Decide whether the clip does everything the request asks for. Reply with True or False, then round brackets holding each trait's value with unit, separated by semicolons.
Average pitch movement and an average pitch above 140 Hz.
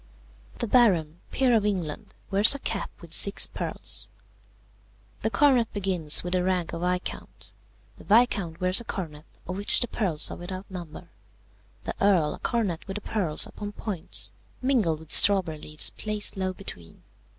True (4.0 semitones; 190 Hz)